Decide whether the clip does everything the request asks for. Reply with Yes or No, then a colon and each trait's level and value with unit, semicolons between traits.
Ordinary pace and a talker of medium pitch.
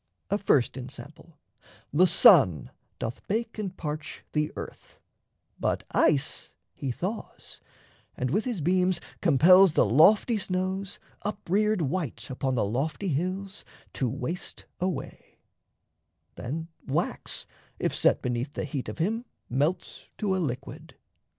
No: slow, 130 wpm; medium, 165 Hz